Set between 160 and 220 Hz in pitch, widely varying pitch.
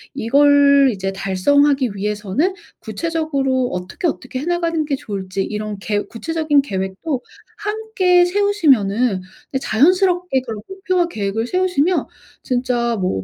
No: very high, 270 Hz; wide, 8.1 semitones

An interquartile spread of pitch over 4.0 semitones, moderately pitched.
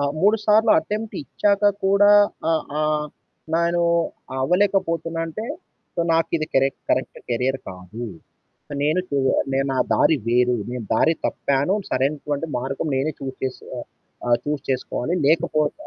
Yes: average, 4.5 semitones; medium, 155 Hz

